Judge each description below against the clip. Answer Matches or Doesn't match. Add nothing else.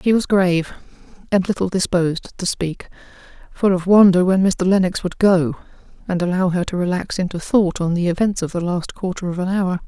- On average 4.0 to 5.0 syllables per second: Doesn't match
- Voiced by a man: Doesn't match